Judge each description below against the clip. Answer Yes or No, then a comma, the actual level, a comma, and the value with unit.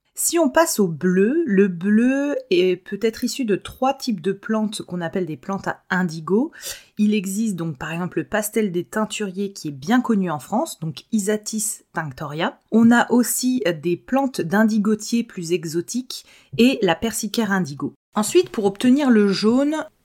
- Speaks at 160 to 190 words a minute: Yes, average, 170 wpm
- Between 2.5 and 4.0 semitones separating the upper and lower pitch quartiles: No, average, 4.4 semitones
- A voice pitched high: Yes, high, 210 Hz